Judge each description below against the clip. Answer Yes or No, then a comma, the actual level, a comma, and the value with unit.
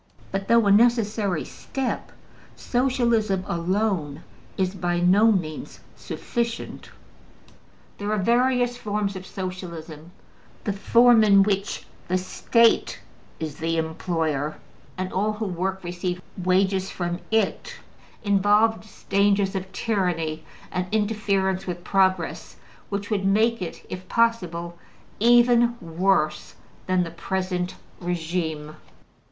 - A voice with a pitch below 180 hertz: No, high, 190 Hz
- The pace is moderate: No, slow, 115 wpm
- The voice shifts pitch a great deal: No, average, 3.4 semitones